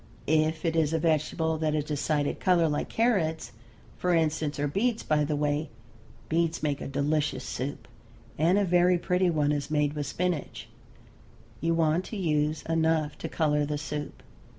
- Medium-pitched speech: Yes, medium, 155 Hz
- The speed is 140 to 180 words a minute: Yes, average, 175 wpm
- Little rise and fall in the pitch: Yes, narrow, 2.1 semitones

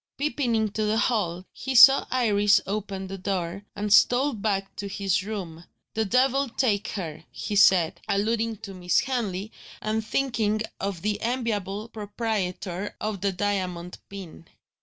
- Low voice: No, high, 205 Hz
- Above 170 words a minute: No, average, 145 wpm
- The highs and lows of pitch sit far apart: No, average, 2.8 semitones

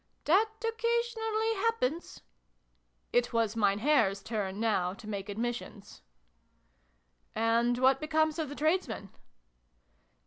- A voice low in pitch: No, high, 240 Hz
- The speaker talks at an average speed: No, slow, 115 wpm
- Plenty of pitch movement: Yes, wide, 7.8 semitones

